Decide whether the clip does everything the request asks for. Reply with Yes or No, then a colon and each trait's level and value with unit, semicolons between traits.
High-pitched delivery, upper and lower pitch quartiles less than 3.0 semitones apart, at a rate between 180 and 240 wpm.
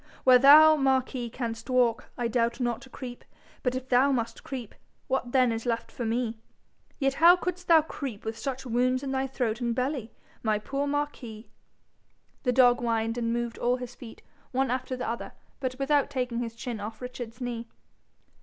Yes: very high, 250 Hz; narrow, 2.4 semitones; average, 185 wpm